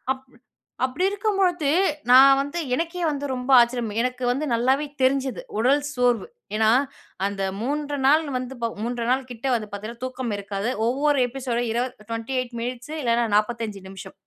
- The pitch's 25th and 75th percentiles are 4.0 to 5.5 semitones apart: No, average, 2.9 semitones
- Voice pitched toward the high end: Yes, very high, 250 Hz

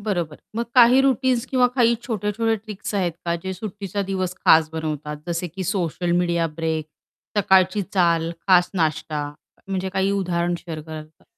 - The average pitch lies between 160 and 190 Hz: Yes, medium, 185 Hz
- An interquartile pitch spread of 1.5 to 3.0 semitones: No, average, 3.8 semitones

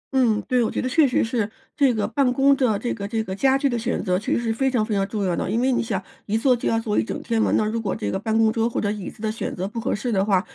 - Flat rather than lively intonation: No, average, 3.0 semitones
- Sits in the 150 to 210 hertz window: No, high, 225 Hz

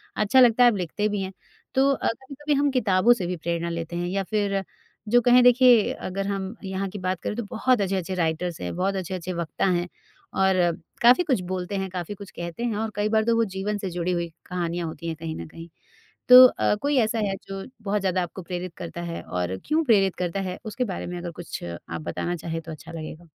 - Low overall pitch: No, high, 190 Hz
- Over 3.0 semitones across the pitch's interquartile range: Yes, average, 4.0 semitones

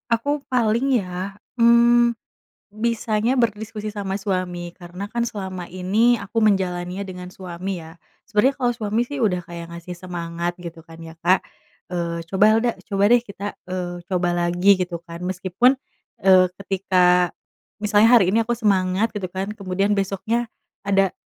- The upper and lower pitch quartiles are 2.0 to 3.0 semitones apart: No, average, 3.6 semitones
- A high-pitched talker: Yes, high, 195 Hz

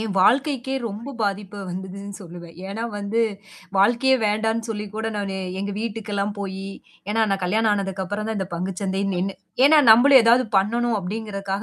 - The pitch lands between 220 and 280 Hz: No, high, 205 Hz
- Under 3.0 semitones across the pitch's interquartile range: Yes, narrow, 2.6 semitones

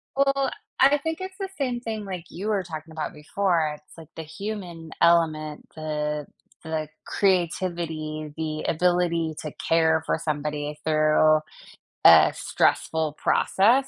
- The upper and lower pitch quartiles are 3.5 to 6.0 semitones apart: Yes, average, 4.1 semitones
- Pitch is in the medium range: Yes, medium, 165 Hz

